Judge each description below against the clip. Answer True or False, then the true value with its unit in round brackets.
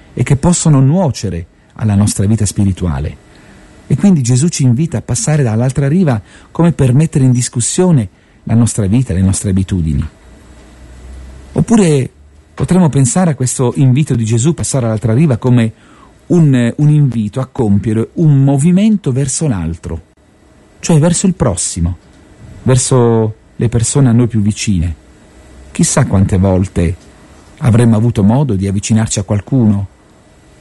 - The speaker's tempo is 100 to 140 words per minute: True (135 wpm)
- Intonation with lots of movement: True (6.3 semitones)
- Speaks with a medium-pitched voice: False (115 Hz)